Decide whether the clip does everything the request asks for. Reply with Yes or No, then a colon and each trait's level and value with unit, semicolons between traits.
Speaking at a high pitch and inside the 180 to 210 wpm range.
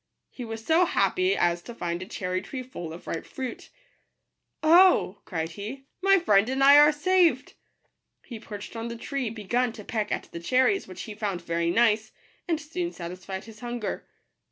Yes: high, 230 Hz; average, 195 wpm